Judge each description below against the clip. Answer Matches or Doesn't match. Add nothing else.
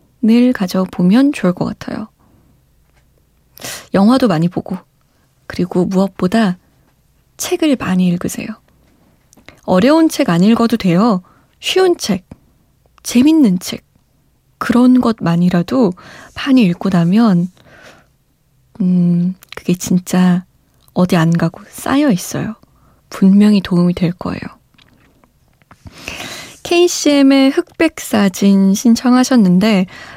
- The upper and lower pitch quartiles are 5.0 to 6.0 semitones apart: Matches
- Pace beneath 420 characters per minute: Matches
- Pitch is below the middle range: Doesn't match